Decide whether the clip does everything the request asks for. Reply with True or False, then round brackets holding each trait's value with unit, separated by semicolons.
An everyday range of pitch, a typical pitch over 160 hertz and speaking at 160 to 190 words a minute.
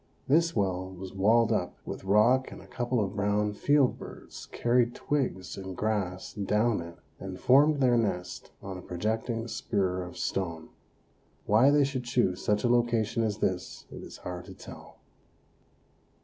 False (4.3 semitones; 105 Hz; 165 wpm)